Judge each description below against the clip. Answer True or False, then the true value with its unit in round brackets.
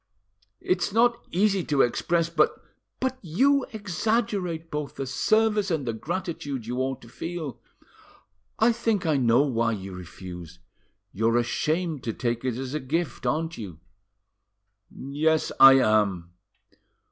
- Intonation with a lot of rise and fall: True (7.3 semitones)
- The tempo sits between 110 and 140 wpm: True (135 wpm)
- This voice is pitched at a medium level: True (150 Hz)